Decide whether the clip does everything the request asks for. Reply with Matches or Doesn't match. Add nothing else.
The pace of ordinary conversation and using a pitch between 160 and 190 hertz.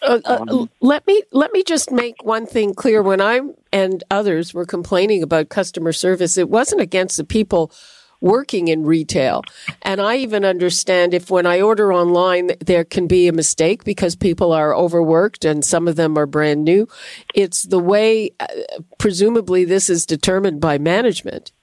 Matches